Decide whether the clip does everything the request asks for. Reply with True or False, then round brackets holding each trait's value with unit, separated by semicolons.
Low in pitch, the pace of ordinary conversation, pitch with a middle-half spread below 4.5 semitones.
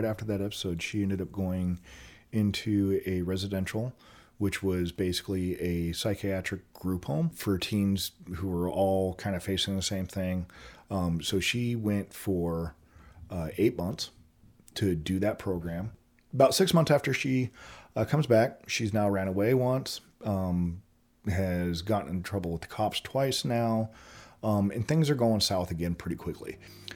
True (95 Hz; 160 wpm; 3.5 semitones)